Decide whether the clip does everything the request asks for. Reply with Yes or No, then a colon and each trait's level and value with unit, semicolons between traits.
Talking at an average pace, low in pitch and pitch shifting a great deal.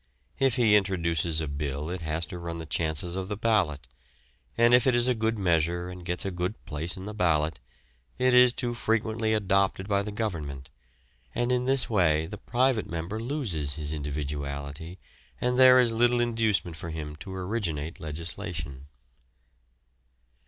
Yes: average, 165 wpm; very low, 90 Hz; wide, 6.1 semitones